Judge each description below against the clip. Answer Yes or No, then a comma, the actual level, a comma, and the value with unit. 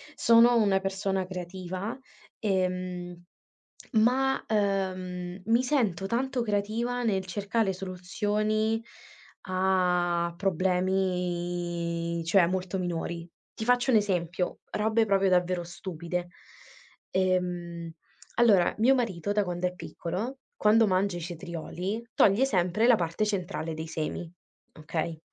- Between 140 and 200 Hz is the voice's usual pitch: Yes, medium, 185 Hz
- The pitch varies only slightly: No, average, 3.3 semitones